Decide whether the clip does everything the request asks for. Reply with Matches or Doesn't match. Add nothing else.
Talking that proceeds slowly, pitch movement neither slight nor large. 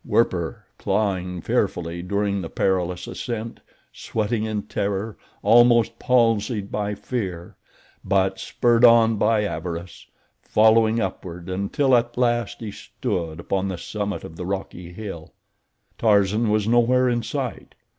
Matches